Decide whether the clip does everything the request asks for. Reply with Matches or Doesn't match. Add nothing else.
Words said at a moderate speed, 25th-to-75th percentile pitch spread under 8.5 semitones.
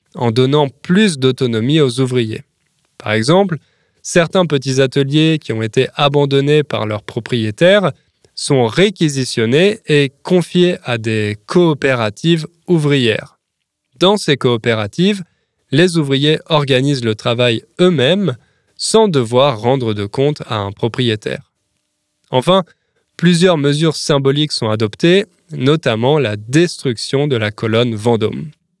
Doesn't match